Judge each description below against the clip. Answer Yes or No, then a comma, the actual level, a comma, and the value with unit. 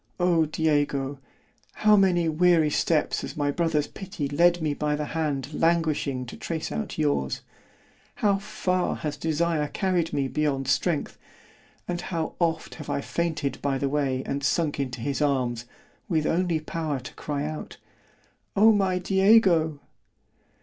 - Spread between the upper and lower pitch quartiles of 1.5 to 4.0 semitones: Yes, average, 3.2 semitones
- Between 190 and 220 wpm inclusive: No, average, 145 wpm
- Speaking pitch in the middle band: Yes, medium, 155 Hz